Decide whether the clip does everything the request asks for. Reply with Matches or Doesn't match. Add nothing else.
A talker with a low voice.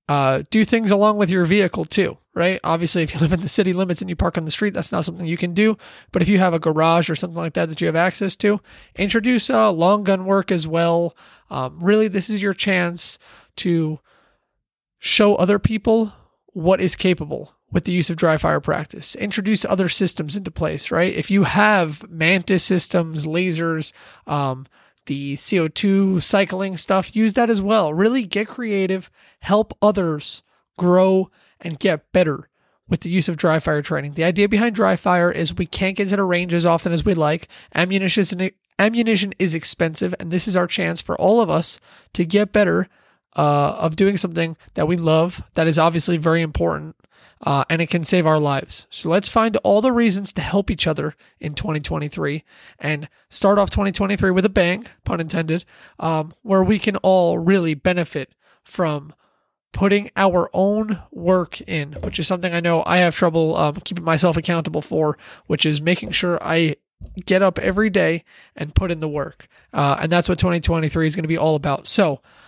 Doesn't match